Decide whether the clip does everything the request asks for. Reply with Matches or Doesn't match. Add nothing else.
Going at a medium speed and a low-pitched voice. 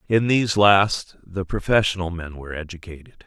Matches